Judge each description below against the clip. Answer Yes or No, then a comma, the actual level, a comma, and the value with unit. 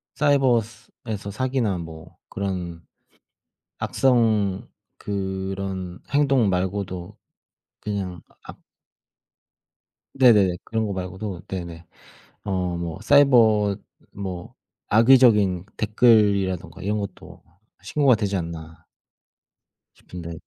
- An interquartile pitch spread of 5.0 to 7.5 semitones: No, average, 3.6 semitones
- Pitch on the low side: Yes, low, 100 Hz